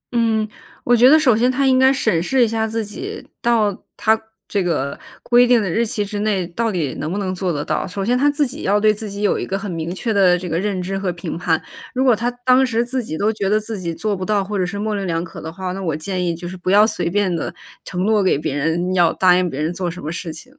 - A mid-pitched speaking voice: No, high, 200 Hz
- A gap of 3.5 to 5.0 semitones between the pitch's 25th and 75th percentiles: Yes, average, 4.1 semitones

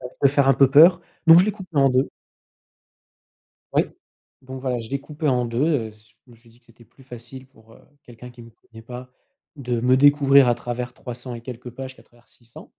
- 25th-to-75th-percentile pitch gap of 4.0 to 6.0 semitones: No, narrow, 2.4 semitones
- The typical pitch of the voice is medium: No, low, 125 Hz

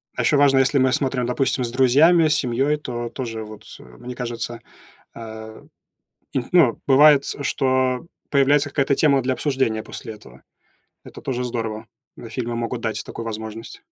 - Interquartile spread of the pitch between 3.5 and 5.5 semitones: No, average, 3.1 semitones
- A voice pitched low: Yes, low, 125 Hz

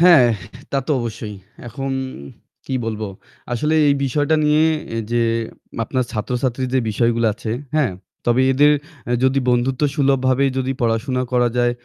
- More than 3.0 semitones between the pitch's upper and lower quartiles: No, narrow, 2.6 semitones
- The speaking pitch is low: Yes, low, 130 Hz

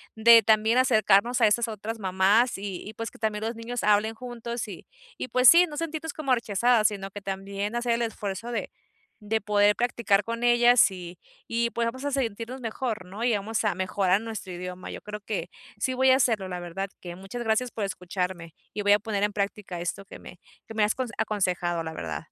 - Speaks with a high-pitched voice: Yes, high, 215 Hz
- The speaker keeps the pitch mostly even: No, average, 3.3 semitones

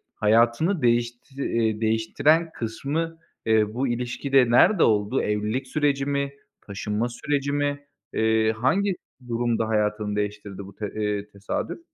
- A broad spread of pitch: No, average, 4.6 semitones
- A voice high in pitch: No, low, 115 Hz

